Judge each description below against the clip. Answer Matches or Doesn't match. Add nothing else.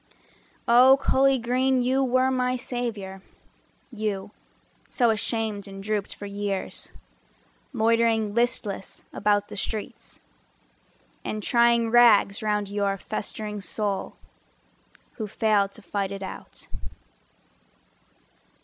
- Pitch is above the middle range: Matches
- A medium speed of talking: Doesn't match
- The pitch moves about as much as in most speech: Matches